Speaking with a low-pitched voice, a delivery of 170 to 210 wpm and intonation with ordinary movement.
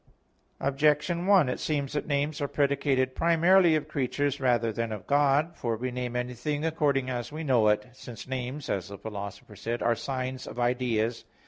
Yes: low, 130 Hz; average, 180 wpm; average, 3.6 semitones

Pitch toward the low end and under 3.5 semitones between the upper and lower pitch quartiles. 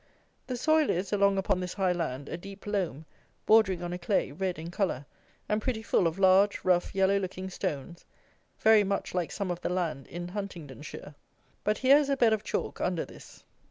No: high, 190 Hz; average, 2.9 semitones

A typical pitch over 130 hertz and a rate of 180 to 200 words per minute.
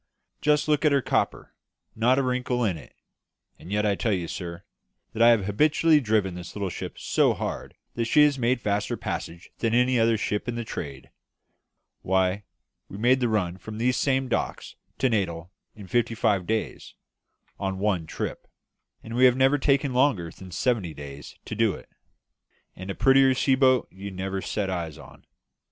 No: low, 110 Hz; average, 185 wpm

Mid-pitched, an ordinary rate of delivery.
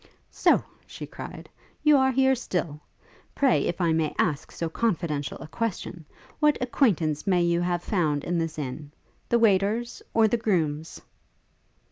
Yes: medium, 175 Hz; average, 150 wpm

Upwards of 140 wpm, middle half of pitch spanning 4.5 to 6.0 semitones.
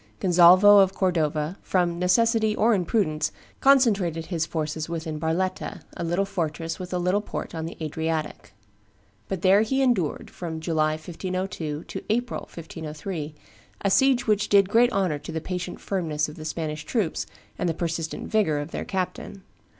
No: average, 165 wpm; average, 3.7 semitones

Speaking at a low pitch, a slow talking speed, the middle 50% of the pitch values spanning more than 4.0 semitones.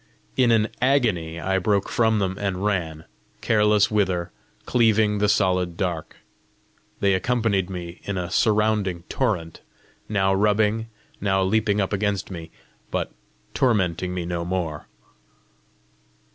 No: low, 100 Hz; slow, 125 wpm; average, 3.0 semitones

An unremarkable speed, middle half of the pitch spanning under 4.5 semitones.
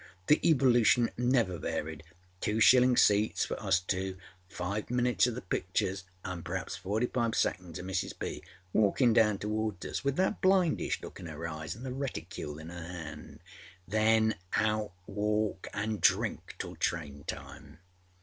No: average, 155 wpm; average, 4.9 semitones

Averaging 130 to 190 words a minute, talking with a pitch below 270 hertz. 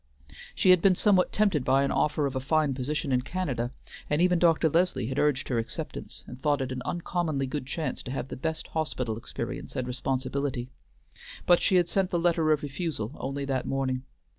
No: average, 200 wpm; medium, 140 Hz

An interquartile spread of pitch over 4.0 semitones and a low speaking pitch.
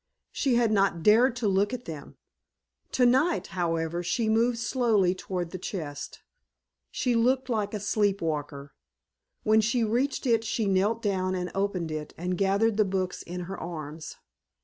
No: average, 4.5 semitones; high, 200 Hz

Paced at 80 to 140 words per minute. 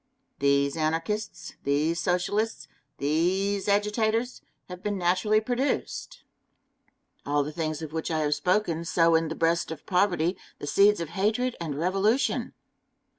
Yes: slow, 135 wpm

